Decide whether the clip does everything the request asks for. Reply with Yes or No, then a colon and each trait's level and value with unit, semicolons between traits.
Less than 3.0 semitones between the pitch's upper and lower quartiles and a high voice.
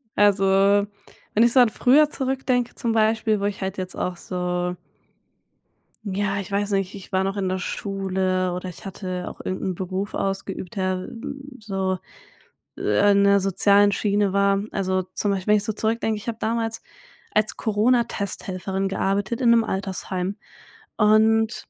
Yes: narrow, 2.4 semitones; high, 200 Hz